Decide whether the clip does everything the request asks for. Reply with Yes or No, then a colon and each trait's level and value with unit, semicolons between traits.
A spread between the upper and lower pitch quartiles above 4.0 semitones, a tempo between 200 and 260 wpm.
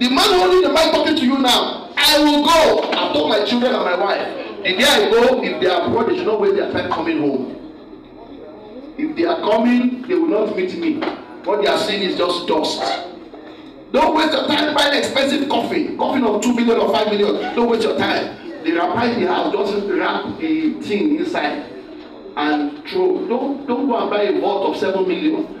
Yes: average, 5.3 semitones; fast, 205 wpm